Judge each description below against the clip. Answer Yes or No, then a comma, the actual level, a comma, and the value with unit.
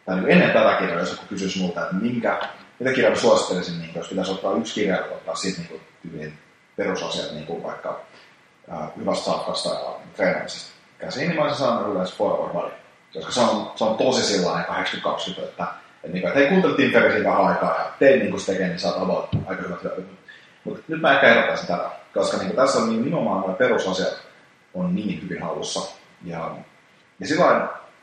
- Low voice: Yes, very low, 95 Hz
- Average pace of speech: No, fast, 165 wpm